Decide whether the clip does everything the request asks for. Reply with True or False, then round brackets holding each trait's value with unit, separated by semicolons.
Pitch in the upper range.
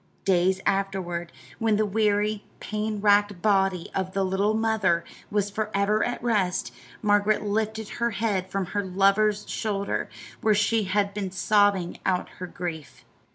True (205 Hz)